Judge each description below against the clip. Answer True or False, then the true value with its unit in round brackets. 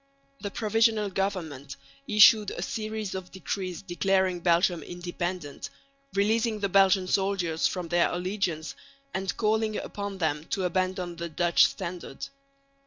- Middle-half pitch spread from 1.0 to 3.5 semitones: True (2.6 semitones)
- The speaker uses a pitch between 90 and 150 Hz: False (185 Hz)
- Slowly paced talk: True (125 wpm)